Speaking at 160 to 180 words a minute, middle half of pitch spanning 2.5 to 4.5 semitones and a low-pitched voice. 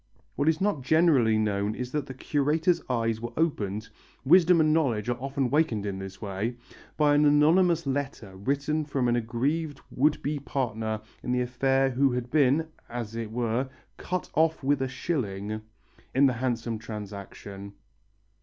No: average, 165 wpm; average, 4.9 semitones; low, 130 Hz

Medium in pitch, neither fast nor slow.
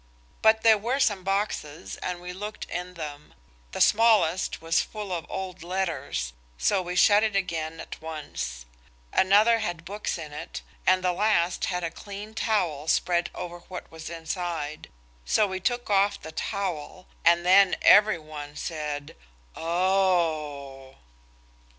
Yes: medium, 180 Hz; average, 145 wpm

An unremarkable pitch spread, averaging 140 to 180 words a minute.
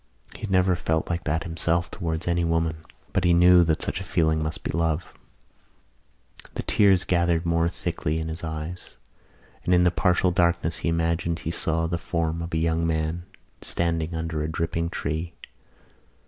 No: narrow, 1.3 semitones; average, 175 wpm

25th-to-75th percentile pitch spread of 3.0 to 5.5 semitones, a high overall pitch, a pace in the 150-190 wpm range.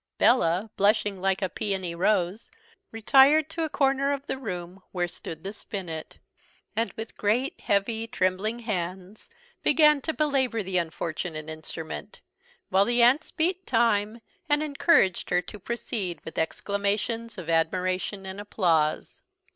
No: average, 4.8 semitones; high, 205 Hz; average, 140 wpm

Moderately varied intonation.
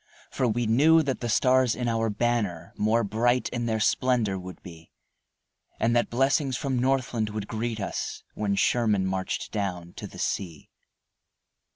Yes: average, 3.4 semitones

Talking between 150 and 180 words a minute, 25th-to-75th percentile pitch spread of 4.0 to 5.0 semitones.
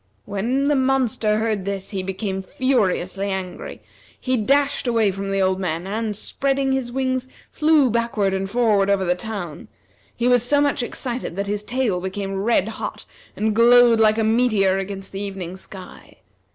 Yes: average, 170 wpm; average, 4.3 semitones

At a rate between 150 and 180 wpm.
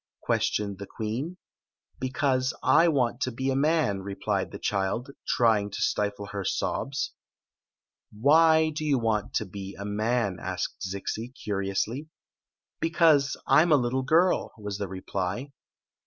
Yes: average, 160 wpm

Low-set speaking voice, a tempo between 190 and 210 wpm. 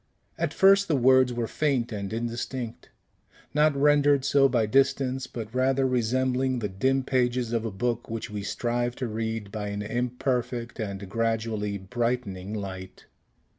No: low, 120 Hz; average, 150 wpm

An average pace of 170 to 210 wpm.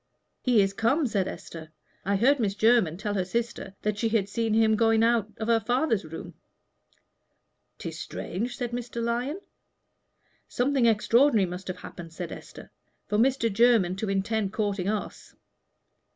No: average, 155 wpm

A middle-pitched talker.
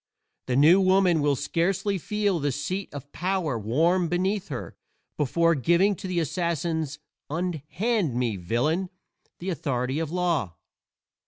Yes: medium, 165 Hz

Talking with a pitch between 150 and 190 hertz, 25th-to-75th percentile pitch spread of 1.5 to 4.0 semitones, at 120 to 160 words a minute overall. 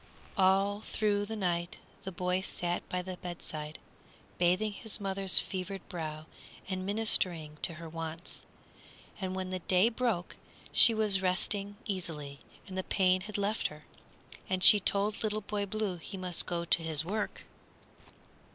Yes: medium, 185 Hz; average, 2.8 semitones; average, 150 wpm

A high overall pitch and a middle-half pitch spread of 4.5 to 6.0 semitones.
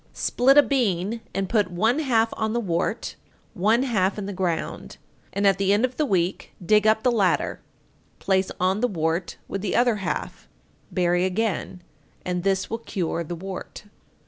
No: high, 195 Hz; average, 3.8 semitones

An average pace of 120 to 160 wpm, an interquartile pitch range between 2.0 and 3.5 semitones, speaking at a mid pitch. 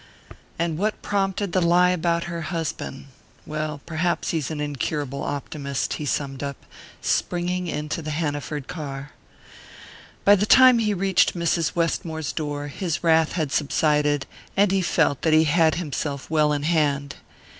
Yes: average, 150 wpm; average, 3.0 semitones; medium, 160 Hz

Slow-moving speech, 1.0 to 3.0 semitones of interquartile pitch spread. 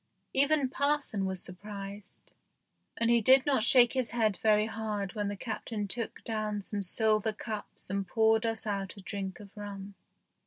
No: average, 165 wpm; narrow, 2.5 semitones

